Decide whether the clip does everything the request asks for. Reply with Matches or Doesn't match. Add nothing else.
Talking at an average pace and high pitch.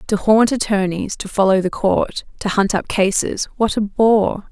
Matches